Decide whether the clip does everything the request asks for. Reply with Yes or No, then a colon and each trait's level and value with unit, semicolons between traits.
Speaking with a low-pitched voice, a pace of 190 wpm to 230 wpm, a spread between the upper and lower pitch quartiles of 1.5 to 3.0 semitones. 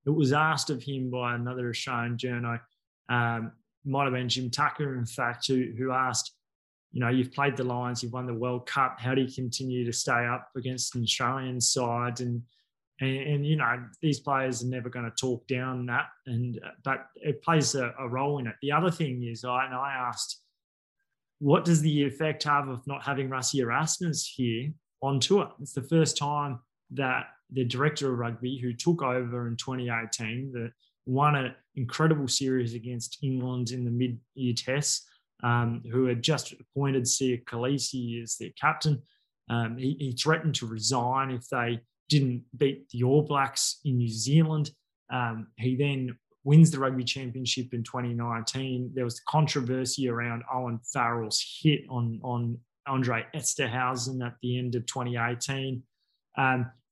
No: low, 130 Hz; average, 175 wpm; narrow, 2.5 semitones